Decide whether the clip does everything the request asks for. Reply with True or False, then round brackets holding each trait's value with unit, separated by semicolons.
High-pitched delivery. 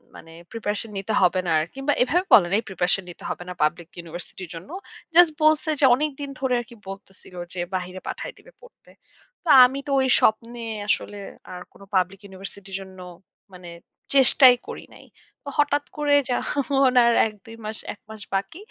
True (215 Hz)